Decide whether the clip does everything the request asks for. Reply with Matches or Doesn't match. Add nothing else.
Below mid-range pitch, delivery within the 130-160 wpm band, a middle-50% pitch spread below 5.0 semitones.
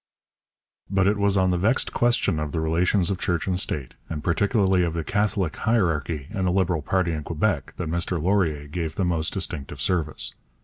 Doesn't match